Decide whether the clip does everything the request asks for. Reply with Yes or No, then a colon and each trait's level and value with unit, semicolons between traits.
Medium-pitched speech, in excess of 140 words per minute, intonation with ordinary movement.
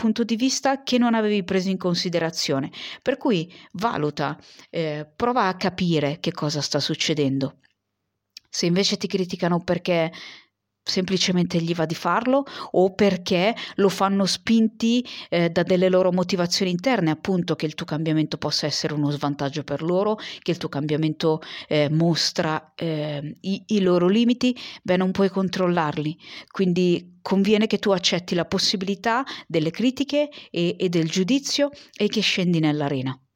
Yes: medium, 180 Hz; average, 150 wpm; average, 4.6 semitones